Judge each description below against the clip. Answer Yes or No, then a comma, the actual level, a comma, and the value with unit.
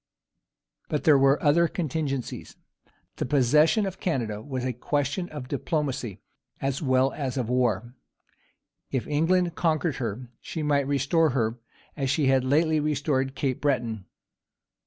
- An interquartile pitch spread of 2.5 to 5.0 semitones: Yes, average, 3.2 semitones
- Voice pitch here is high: No, medium, 140 Hz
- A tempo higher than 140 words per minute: No, slow, 135 wpm